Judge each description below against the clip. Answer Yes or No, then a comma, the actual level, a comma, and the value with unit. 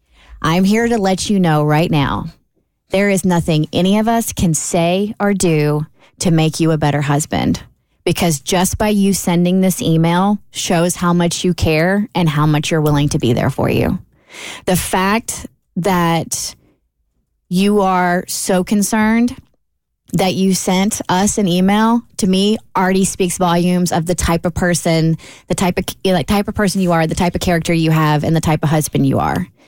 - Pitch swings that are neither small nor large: Yes, average, 3.4 semitones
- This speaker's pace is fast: No, average, 185 wpm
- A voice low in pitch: No, medium, 175 Hz